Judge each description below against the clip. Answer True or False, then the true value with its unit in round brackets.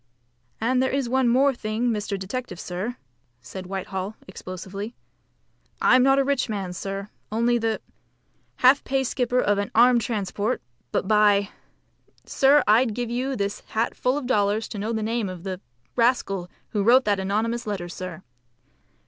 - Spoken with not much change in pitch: False (4.0 semitones)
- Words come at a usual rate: True (160 wpm)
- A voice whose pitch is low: False (220 Hz)